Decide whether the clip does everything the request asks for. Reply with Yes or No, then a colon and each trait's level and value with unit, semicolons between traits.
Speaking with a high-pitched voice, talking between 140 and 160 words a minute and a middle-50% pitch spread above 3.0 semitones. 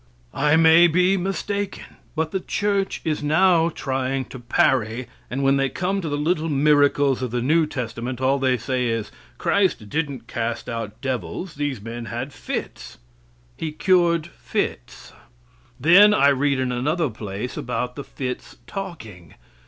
No: medium, 140 Hz; average, 150 wpm; average, 5.1 semitones